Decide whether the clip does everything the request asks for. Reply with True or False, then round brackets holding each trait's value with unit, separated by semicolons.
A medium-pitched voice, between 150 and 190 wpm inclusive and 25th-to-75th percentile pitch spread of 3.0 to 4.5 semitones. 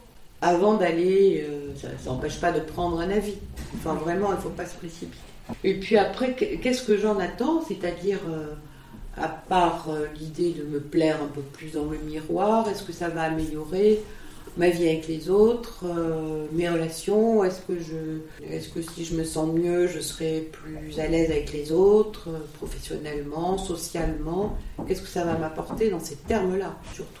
True (170 Hz; 180 wpm; 3.4 semitones)